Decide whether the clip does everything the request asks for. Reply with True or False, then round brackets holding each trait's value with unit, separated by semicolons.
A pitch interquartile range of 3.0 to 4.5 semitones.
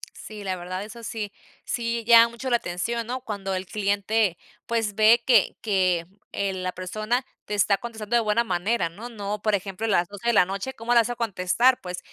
True (3.4 semitones)